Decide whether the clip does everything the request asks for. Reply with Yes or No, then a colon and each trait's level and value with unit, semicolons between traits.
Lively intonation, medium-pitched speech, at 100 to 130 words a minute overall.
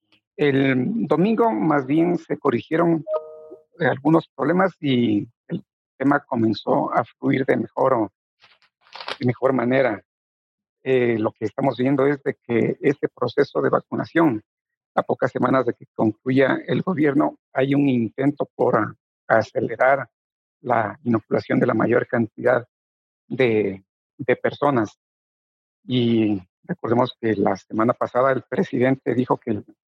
No: wide, 5.7 semitones; low, 130 Hz; slow, 125 wpm